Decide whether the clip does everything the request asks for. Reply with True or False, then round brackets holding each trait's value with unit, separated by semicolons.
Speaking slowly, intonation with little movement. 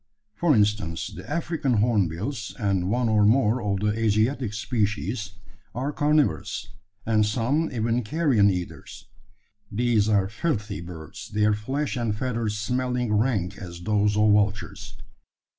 False (130 wpm; 3.2 semitones)